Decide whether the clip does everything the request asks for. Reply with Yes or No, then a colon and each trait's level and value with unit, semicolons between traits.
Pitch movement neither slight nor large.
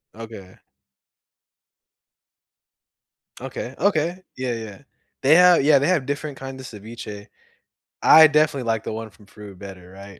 No: wide, 6.5 semitones